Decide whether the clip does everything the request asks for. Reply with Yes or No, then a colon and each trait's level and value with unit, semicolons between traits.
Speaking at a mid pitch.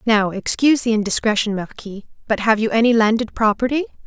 No: high, 220 Hz